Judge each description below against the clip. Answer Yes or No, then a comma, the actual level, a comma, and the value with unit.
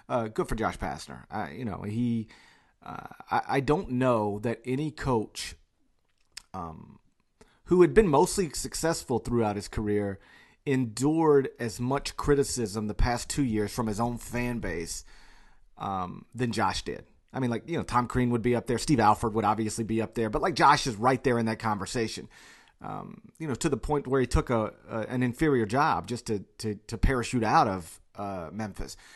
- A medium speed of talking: Yes, average, 190 wpm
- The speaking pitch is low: Yes, low, 120 Hz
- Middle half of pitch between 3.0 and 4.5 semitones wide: Yes, average, 3.5 semitones